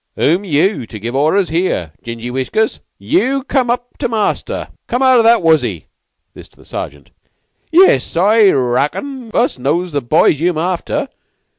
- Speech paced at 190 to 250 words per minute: No, average, 170 wpm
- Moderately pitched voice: Yes, medium, 175 Hz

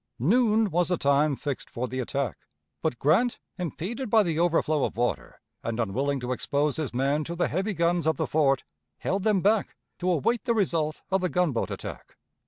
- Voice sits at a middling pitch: Yes, medium, 160 Hz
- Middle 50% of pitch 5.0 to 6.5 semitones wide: Yes, average, 5.3 semitones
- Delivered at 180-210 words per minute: Yes, average, 190 wpm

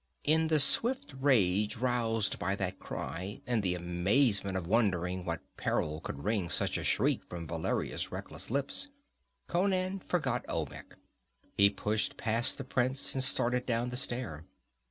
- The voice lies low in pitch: Yes, low, 115 Hz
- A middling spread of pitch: No, wide, 6.1 semitones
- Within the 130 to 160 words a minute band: Yes, average, 150 wpm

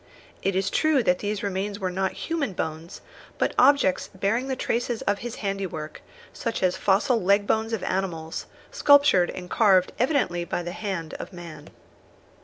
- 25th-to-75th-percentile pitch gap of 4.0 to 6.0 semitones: Yes, average, 4.3 semitones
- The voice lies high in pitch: Yes, high, 195 Hz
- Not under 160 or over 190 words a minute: Yes, average, 165 wpm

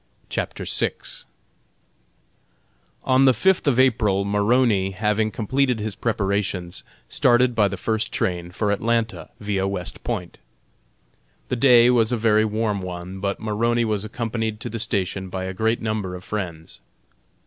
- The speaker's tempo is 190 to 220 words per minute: No, average, 145 wpm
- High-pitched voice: No, low, 105 Hz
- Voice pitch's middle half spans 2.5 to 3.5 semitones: Yes, average, 3.2 semitones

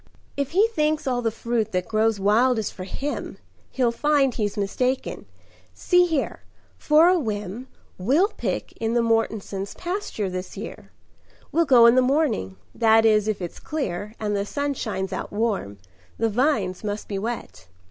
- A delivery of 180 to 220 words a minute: No, average, 170 wpm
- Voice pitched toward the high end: Yes, high, 225 Hz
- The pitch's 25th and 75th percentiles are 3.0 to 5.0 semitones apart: No, wide, 5.4 semitones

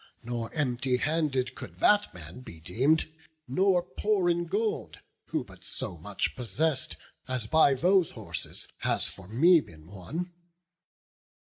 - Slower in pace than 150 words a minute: Yes, slow, 135 wpm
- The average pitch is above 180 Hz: No, low, 135 Hz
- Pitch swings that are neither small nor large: No, wide, 7.2 semitones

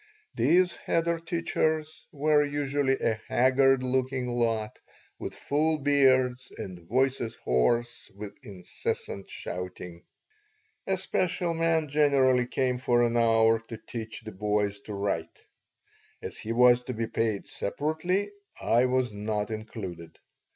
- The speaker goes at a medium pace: No, slow, 125 wpm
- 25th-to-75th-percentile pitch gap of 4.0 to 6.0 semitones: Yes, average, 4.9 semitones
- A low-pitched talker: Yes, low, 125 Hz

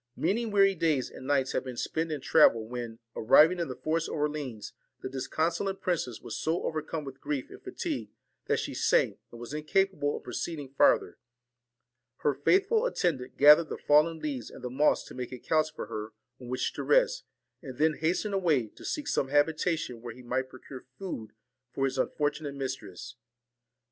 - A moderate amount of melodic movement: Yes, average, 4.3 semitones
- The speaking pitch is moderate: Yes, medium, 145 Hz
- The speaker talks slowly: No, average, 185 wpm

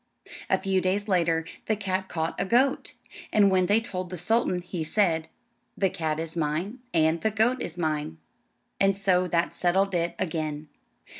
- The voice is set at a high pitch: No, medium, 180 Hz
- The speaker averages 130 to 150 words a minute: No, average, 170 wpm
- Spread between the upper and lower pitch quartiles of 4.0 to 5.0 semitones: No, average, 3.5 semitones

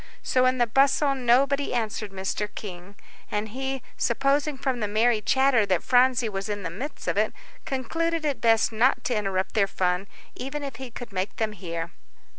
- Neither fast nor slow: Yes, average, 185 wpm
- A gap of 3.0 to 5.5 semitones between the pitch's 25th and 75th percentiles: Yes, average, 4.6 semitones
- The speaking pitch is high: Yes, high, 235 Hz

